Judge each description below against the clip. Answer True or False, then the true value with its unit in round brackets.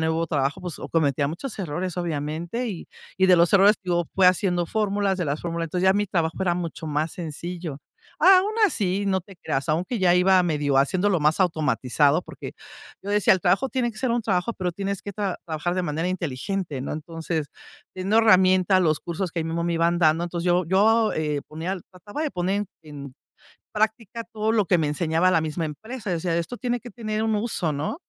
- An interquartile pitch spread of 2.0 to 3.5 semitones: False (3.9 semitones)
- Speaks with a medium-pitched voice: True (180 Hz)